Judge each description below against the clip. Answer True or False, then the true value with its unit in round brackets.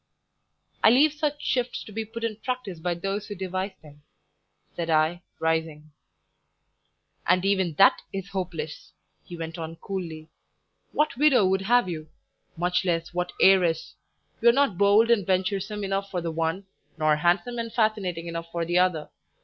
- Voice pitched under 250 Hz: True (185 Hz)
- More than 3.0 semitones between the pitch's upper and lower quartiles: True (4.2 semitones)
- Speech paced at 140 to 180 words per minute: True (160 wpm)